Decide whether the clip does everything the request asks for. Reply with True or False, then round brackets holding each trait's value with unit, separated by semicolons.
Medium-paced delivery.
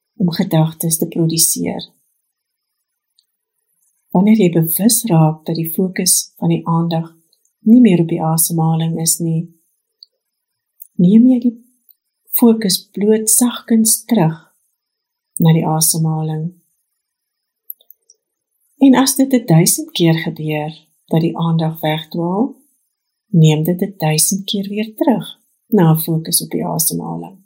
False (120 wpm)